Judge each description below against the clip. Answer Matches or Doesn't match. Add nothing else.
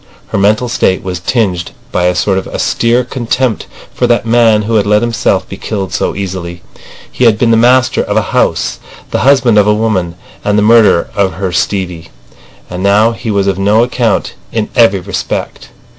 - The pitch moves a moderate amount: Matches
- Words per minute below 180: Doesn't match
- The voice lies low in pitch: Matches